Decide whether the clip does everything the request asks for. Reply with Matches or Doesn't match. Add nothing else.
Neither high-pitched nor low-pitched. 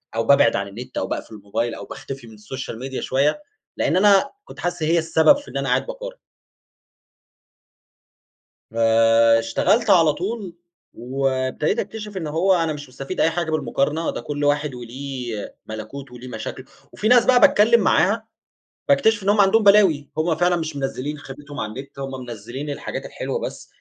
Matches